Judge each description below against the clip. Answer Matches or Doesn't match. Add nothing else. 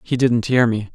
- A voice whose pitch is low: Matches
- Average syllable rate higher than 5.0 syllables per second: Doesn't match